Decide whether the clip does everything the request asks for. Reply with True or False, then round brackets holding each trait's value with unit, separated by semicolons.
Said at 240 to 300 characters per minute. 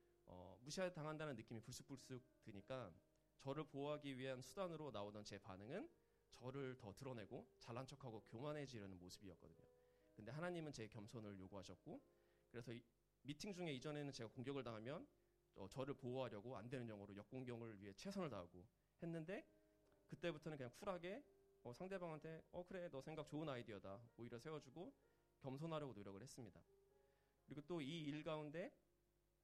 False (370 characters per minute)